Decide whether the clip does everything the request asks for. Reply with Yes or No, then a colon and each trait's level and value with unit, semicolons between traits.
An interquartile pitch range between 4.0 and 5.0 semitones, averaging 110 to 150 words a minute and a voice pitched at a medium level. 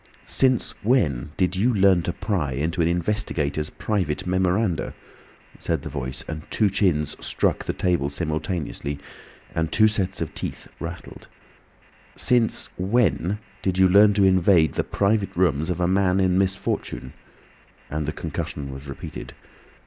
No: average, 4.3 semitones; average, 145 wpm; very low, 90 Hz